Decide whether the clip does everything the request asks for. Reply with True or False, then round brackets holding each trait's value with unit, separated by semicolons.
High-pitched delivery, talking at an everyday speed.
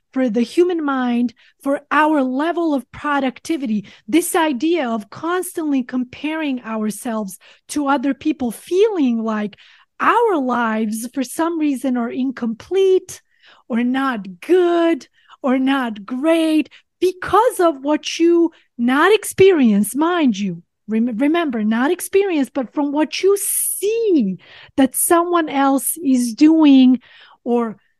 False (280 Hz; 120 wpm)